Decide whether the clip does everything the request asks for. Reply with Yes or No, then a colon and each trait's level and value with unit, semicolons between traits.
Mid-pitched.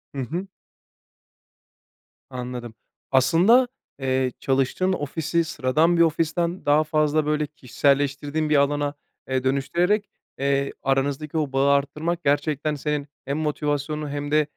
Yes: medium, 145 Hz